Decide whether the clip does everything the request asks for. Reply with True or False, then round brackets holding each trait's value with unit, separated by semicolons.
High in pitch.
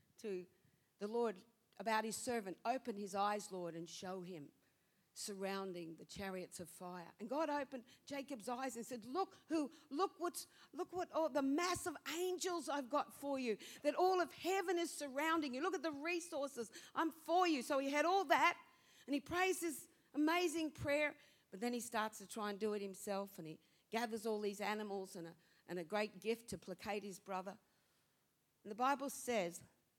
True (240 Hz)